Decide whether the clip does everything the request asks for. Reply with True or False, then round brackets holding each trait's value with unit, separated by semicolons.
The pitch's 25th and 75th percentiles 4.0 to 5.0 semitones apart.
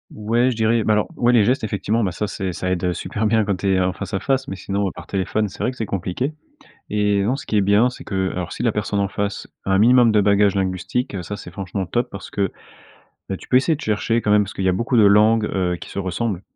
False (2.9 semitones)